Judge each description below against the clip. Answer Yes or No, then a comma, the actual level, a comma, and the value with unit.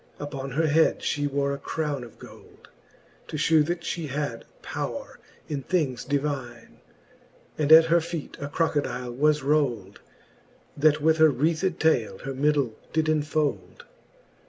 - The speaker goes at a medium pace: Yes, average, 145 wpm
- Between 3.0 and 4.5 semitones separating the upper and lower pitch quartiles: No, narrow, 2.6 semitones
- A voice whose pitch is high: No, medium, 145 Hz